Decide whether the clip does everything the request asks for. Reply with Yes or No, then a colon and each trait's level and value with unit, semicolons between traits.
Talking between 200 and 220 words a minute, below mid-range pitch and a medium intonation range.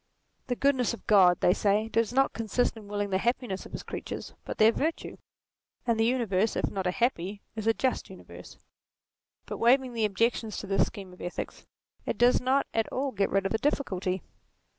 No: fast, 205 wpm; high, 225 Hz; average, 3.9 semitones